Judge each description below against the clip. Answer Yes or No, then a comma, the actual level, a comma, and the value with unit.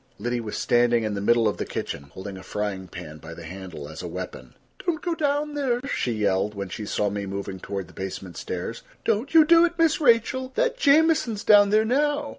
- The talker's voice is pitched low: Yes, low, 115 Hz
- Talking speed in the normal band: No, fast, 220 wpm